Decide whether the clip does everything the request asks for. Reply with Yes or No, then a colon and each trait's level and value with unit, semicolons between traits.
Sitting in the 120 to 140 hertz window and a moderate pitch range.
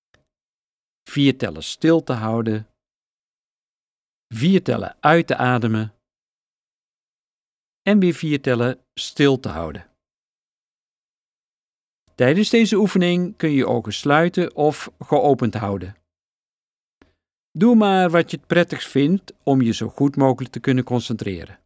No: low, 135 Hz; wide, 6.5 semitones